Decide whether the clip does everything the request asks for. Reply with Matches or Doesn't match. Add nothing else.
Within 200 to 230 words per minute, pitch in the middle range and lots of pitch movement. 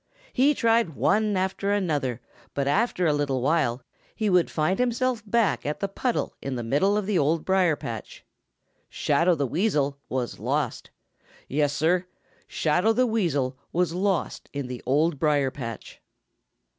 Doesn't match